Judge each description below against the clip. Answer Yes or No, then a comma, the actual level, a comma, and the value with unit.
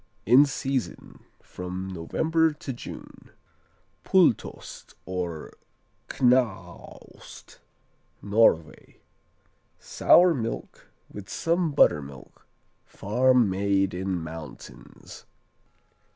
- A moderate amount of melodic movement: No, wide, 6.7 semitones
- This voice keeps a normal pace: No, slow, 70 wpm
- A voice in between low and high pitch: No, low, 105 Hz